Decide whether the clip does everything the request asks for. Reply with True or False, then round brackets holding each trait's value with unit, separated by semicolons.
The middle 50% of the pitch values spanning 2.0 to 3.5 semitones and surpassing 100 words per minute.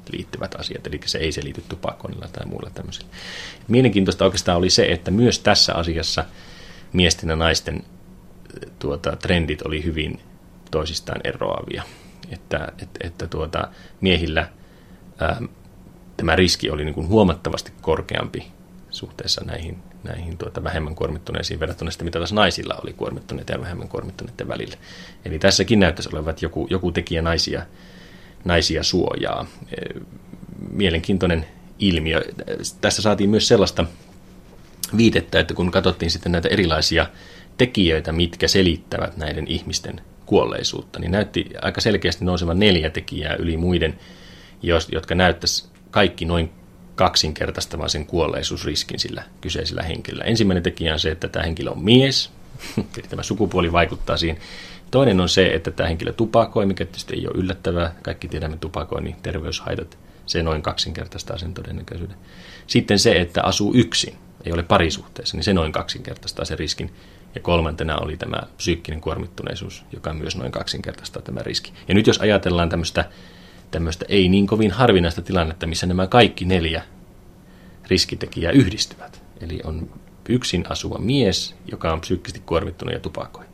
True (2.9 semitones; 140 wpm)